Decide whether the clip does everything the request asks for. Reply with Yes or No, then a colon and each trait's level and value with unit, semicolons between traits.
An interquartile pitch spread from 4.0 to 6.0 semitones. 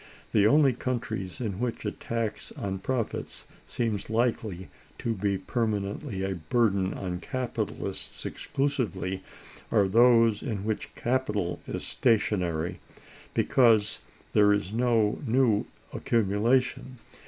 No: average, 3.5 semitones